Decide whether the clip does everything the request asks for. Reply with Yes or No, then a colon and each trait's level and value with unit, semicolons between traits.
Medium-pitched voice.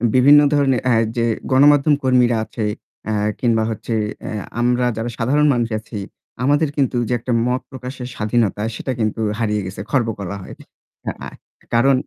No: low, 125 Hz